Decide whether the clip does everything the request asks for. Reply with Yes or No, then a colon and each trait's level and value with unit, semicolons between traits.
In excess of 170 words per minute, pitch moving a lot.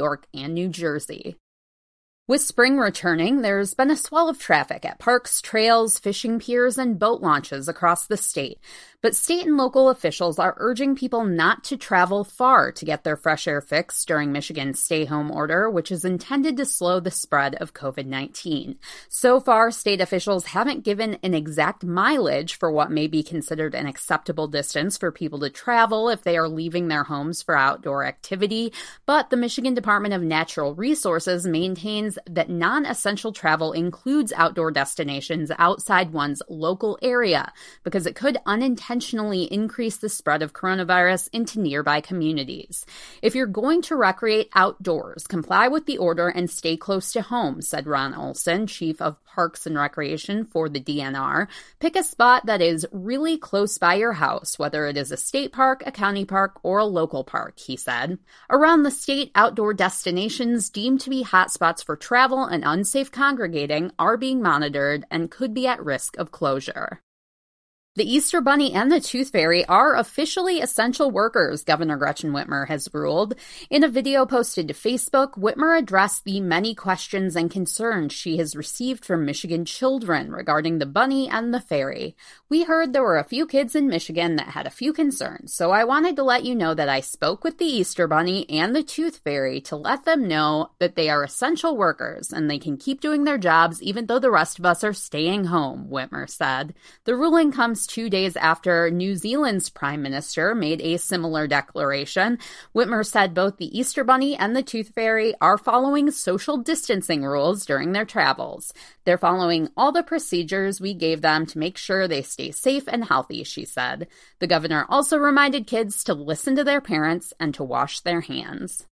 Yes: average, 180 wpm; wide, 7.6 semitones